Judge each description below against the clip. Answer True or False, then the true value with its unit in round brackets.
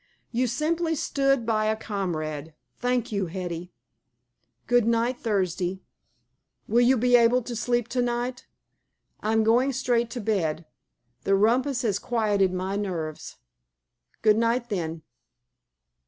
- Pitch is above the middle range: True (225 Hz)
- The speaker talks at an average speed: False (125 wpm)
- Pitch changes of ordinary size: True (4.2 semitones)